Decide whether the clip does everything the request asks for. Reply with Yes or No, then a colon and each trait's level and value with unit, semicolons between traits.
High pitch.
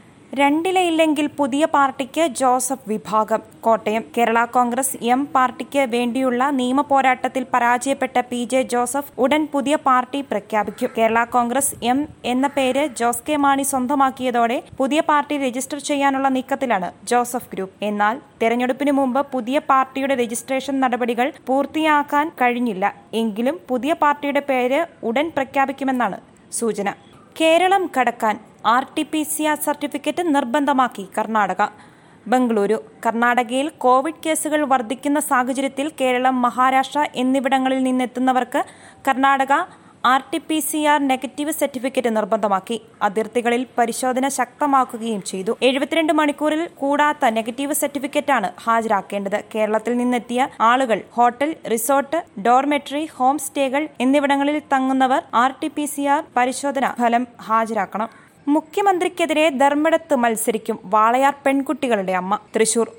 Yes: very high, 265 Hz